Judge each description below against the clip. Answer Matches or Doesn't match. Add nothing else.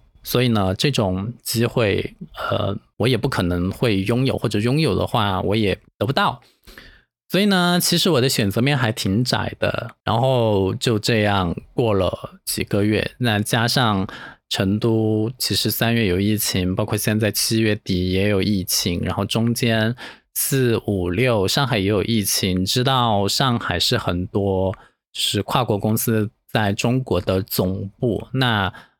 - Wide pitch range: Doesn't match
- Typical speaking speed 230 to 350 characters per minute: Doesn't match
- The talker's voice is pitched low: Matches